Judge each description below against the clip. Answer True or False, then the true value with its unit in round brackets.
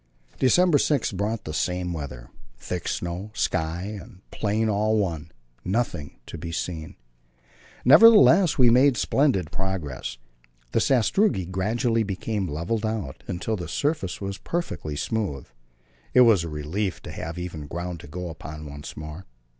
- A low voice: True (95 Hz)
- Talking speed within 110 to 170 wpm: True (145 wpm)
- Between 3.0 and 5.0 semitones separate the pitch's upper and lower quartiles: False (5.6 semitones)